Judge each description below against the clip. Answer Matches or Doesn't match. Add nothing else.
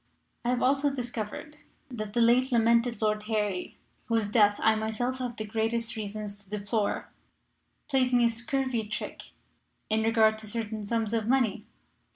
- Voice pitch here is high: Matches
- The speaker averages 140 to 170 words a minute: Matches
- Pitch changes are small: Matches